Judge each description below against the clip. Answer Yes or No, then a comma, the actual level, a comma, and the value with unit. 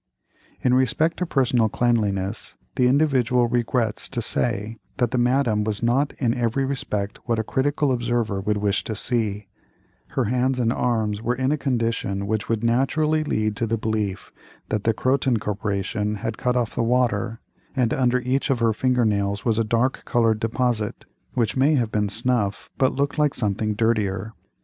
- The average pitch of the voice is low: Yes, low, 115 Hz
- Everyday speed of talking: Yes, average, 175 wpm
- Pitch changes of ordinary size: Yes, average, 3.0 semitones